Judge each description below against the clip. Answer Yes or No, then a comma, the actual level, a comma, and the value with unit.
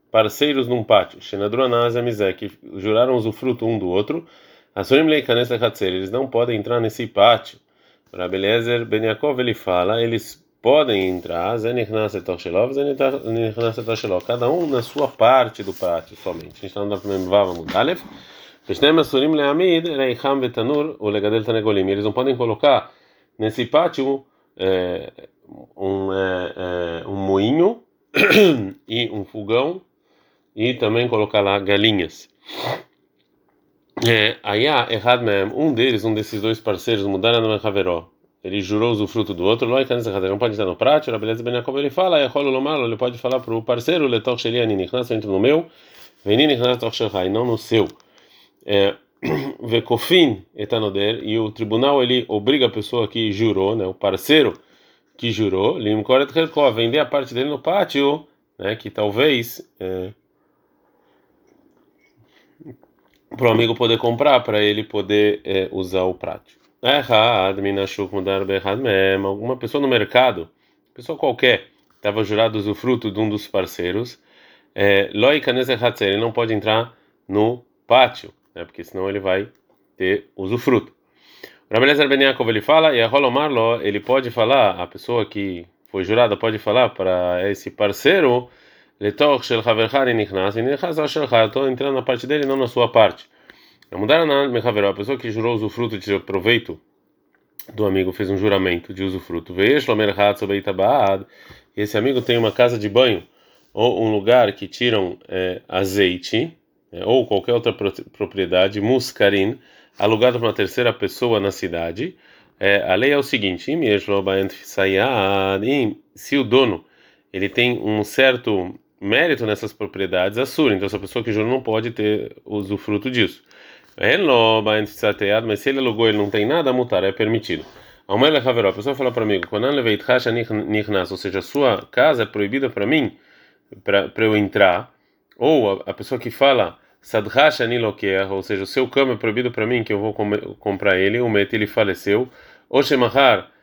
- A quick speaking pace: No, average, 140 wpm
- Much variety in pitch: No, average, 3.8 semitones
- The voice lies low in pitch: Yes, low, 110 Hz